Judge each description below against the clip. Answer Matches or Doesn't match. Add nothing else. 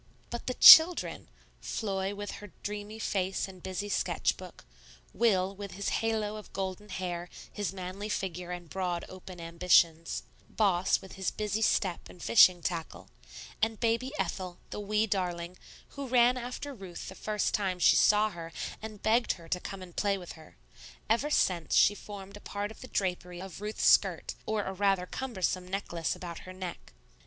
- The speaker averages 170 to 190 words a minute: Matches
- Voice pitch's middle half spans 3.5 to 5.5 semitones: Doesn't match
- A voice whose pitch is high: Matches